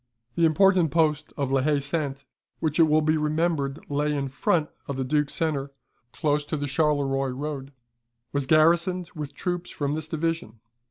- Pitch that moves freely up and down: No, narrow, 2.4 semitones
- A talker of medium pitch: Yes, medium, 150 Hz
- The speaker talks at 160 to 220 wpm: Yes, average, 170 wpm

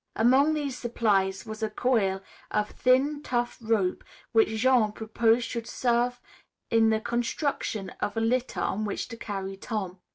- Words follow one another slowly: No, average, 155 wpm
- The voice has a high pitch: Yes, high, 225 Hz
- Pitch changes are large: No, average, 2.7 semitones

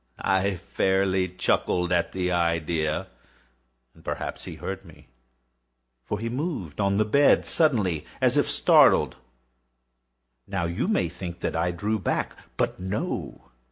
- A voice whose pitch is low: Yes, very low, 95 Hz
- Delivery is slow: Yes, slow, 130 wpm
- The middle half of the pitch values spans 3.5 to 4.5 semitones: No, average, 3.0 semitones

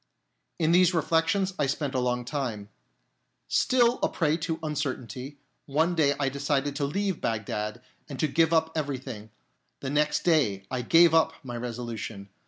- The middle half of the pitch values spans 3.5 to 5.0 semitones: Yes, average, 4.7 semitones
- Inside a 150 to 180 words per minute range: Yes, average, 165 wpm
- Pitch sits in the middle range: Yes, medium, 145 Hz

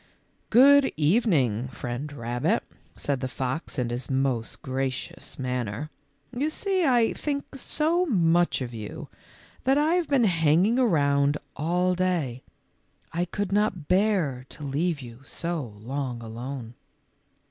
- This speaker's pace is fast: No, slow, 135 wpm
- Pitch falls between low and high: Yes, medium, 150 Hz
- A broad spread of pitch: Yes, wide, 8.4 semitones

